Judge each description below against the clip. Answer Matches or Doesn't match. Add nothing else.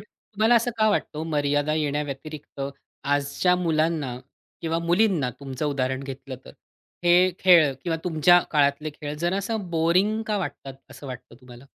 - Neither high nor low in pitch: Matches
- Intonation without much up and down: Doesn't match